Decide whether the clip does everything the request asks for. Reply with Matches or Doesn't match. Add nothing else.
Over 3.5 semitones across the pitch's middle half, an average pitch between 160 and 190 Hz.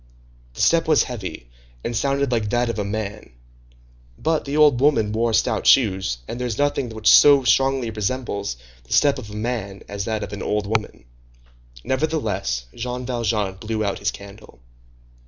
Doesn't match